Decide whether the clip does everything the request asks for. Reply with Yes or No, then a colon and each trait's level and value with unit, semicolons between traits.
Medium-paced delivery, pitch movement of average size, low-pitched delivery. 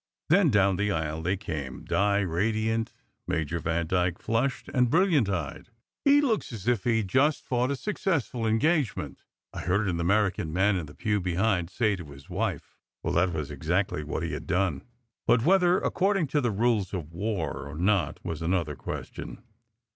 No: average, 175 wpm; wide, 6.2 semitones; low, 100 Hz